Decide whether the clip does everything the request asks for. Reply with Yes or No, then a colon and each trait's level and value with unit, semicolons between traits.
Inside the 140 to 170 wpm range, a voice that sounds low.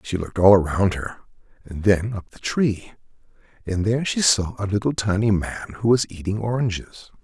No: average, 180 wpm; low, 100 Hz